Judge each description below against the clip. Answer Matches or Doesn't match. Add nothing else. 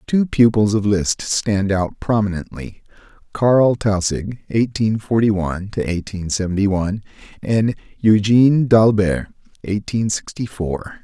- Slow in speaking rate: Matches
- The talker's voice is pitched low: Matches